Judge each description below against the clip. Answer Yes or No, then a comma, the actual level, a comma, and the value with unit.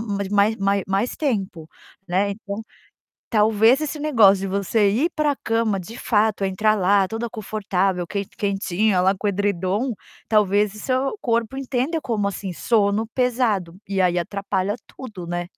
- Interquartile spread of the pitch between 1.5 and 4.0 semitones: Yes, average, 2.9 semitones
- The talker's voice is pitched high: Yes, high, 205 Hz